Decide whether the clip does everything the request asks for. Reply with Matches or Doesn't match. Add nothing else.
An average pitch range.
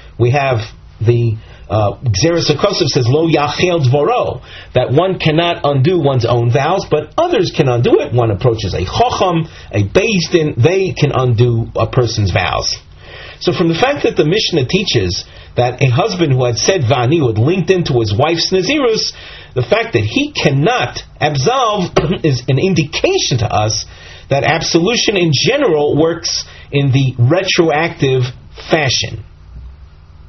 Doesn't match